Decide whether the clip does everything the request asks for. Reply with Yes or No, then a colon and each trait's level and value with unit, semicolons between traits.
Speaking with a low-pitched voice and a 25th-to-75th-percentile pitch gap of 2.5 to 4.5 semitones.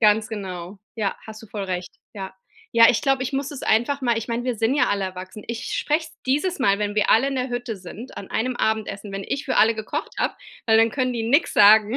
No: high, 225 Hz; average, 3.8 semitones